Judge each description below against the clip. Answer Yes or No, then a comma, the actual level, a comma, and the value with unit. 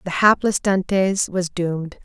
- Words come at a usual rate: Yes, average, 145 wpm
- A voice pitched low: No, medium, 185 Hz